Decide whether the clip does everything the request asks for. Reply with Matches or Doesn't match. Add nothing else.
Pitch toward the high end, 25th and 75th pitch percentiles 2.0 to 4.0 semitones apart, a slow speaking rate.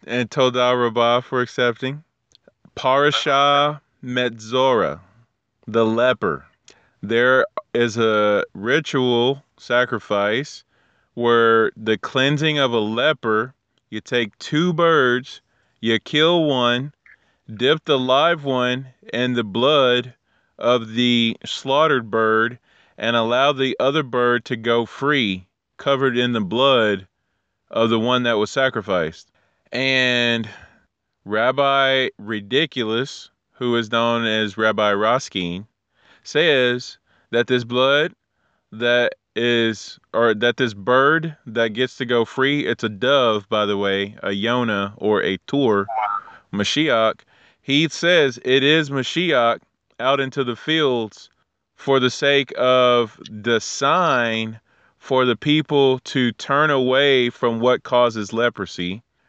Doesn't match